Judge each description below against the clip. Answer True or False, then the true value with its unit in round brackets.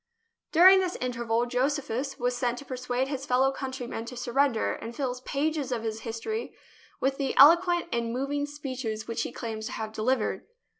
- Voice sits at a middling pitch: False (255 Hz)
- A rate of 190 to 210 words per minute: False (180 wpm)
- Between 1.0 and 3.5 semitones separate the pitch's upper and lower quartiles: True (3.1 semitones)